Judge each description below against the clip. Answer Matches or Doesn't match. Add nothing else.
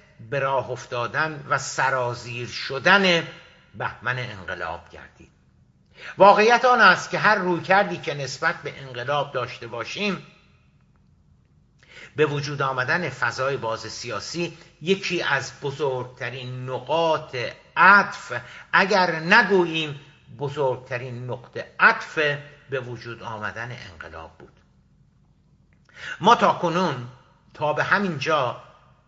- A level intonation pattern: Doesn't match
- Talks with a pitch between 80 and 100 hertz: Doesn't match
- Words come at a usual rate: Doesn't match